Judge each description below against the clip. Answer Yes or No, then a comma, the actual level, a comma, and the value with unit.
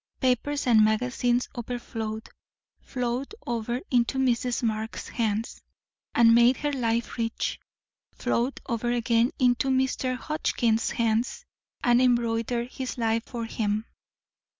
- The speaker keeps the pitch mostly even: Yes, narrow, 1.7 semitones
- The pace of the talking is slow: Yes, slow, 115 wpm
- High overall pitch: Yes, high, 240 Hz